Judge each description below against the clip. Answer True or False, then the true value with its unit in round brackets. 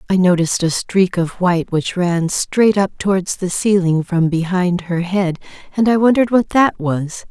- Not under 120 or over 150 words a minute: False (190 wpm)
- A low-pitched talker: False (185 Hz)